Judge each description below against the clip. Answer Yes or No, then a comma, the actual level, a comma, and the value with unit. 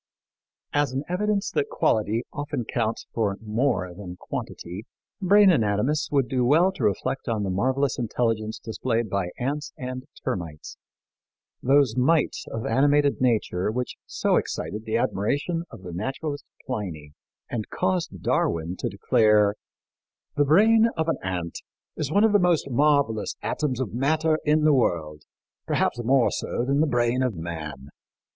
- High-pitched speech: No, low, 125 Hz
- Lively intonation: Yes, wide, 5.9 semitones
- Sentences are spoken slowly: No, average, 150 wpm